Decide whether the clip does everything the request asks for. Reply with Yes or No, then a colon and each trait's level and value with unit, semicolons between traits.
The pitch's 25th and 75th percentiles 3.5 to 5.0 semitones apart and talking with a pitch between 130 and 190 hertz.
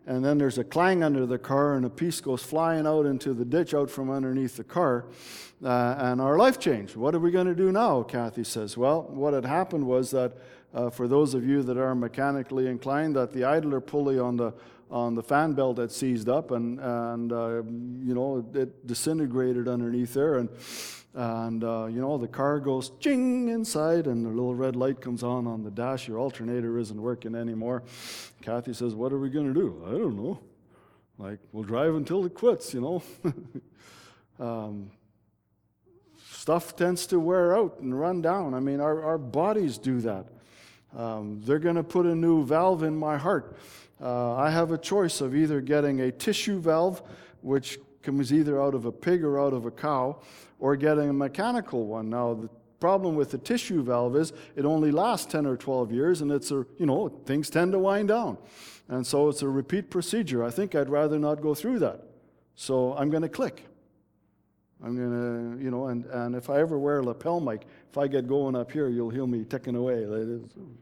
Yes: average, 4.1 semitones; low, 135 Hz